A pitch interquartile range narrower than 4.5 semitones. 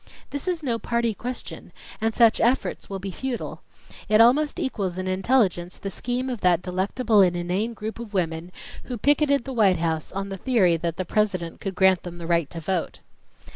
No: average, 5.0 semitones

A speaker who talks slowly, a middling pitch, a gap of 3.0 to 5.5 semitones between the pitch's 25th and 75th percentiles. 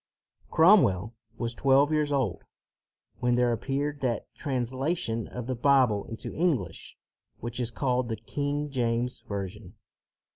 No: slow, 125 wpm; low, 125 Hz; average, 3.8 semitones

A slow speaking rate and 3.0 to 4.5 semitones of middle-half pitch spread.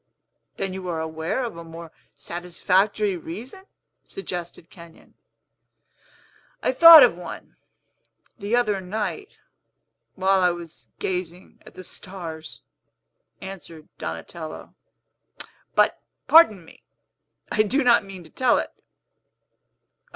Yes: slow, 110 wpm; average, 4.1 semitones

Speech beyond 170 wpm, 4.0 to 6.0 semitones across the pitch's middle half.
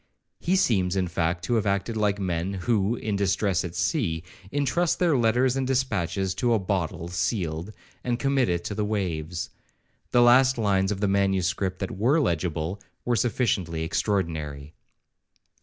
No: average, 155 wpm; average, 5.3 semitones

